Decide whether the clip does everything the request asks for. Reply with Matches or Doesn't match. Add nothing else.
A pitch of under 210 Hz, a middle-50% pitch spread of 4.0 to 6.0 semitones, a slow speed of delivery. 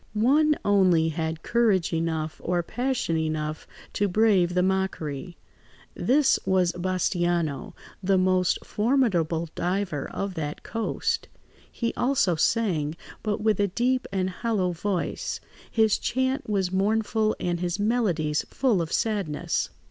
Matches